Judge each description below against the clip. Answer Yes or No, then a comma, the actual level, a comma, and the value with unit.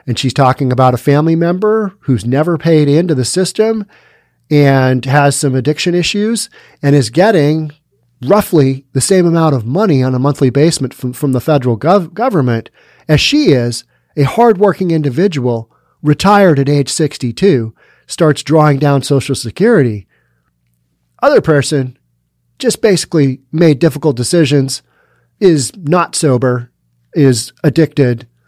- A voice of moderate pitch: Yes, medium, 145 Hz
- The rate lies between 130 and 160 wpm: Yes, slow, 135 wpm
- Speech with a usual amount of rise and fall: Yes, average, 4.6 semitones